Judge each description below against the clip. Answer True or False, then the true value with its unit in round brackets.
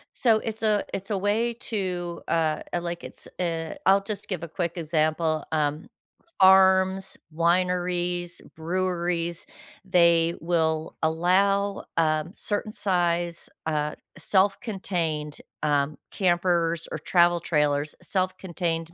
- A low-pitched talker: False (175 Hz)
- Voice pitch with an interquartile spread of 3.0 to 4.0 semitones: False (2.6 semitones)